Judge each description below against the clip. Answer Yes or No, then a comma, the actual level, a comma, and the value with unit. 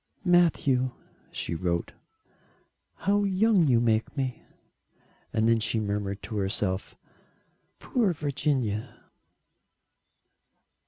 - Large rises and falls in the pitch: Yes, wide, 7.8 semitones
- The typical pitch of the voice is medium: No, low, 120 Hz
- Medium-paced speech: No, slow, 90 wpm